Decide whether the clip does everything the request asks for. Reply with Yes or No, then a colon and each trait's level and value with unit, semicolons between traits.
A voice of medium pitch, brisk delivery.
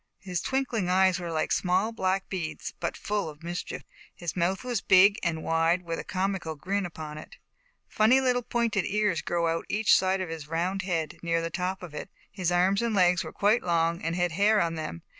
Yes: medium, 180 Hz; fast, 215 wpm